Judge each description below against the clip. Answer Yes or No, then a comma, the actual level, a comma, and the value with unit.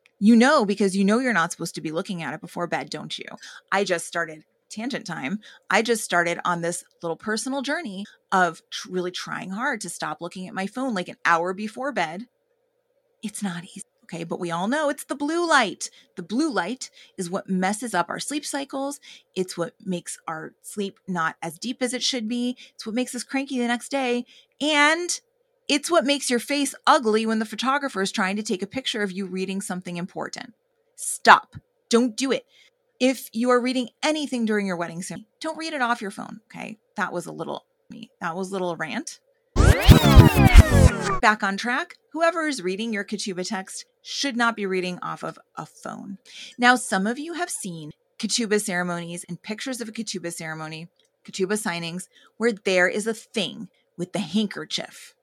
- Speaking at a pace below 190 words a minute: No, average, 195 wpm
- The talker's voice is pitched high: Yes, high, 220 Hz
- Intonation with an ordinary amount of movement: No, wide, 6.0 semitones